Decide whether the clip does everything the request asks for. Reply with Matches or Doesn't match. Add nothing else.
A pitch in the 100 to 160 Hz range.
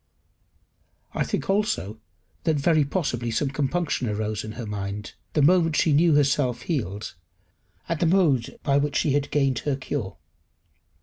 Matches